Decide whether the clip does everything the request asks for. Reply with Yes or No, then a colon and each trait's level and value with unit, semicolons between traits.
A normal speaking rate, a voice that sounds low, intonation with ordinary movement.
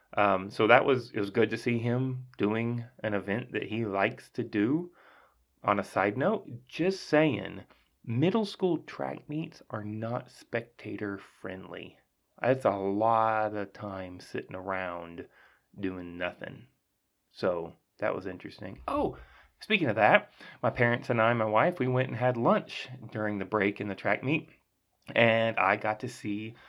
Yes: average, 165 wpm; low, 110 Hz; average, 3.9 semitones